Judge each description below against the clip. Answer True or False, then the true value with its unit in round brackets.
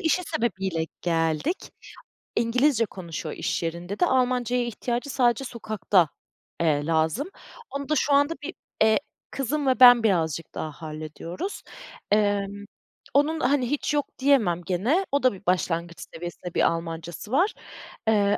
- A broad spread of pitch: True (7.6 semitones)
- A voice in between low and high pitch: False (215 Hz)